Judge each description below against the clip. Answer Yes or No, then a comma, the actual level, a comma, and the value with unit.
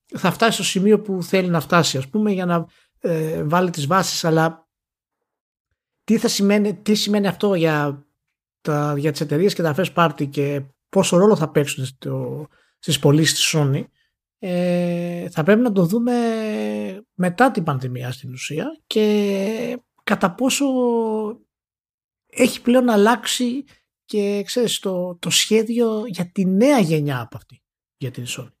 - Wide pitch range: Yes, wide, 5.8 semitones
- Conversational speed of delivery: Yes, average, 150 wpm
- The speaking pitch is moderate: Yes, medium, 180 Hz